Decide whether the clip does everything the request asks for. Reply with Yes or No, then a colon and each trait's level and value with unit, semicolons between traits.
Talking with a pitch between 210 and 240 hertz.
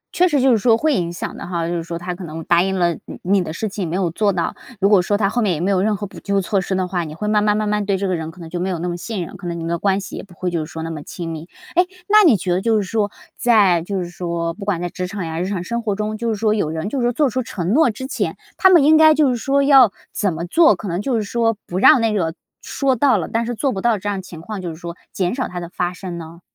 No: high, 195 Hz